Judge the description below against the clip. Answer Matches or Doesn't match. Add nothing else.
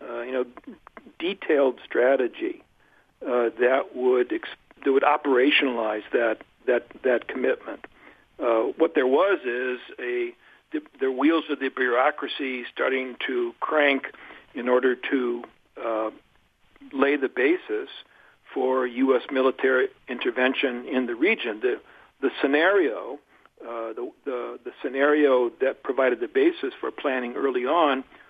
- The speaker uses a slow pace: Matches